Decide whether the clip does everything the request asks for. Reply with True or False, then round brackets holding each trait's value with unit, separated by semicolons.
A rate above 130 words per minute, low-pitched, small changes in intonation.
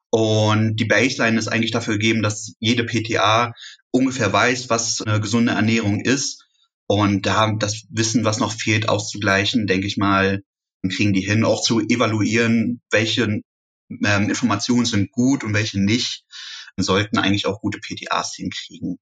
True (160 wpm; 110 Hz; 2.3 semitones)